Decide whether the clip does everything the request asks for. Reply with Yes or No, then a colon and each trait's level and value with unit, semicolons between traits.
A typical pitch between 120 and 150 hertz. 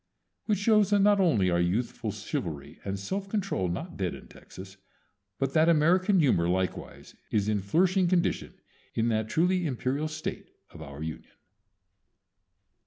Yes: medium, 140 Hz